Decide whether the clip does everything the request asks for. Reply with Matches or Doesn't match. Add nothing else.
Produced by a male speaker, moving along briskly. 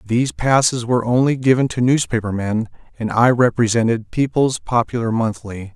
Doesn't match